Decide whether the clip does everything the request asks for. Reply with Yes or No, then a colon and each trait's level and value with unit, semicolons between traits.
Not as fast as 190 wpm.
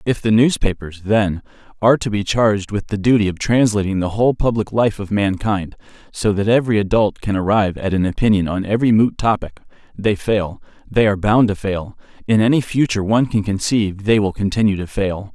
No: average, 195 wpm